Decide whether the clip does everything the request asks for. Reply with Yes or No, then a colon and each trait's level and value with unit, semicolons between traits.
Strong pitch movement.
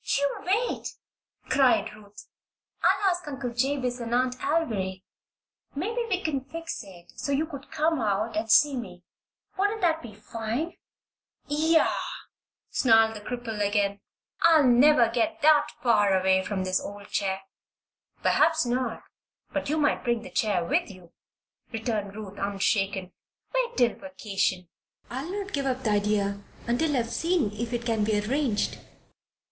Yes: wide, 6.2 semitones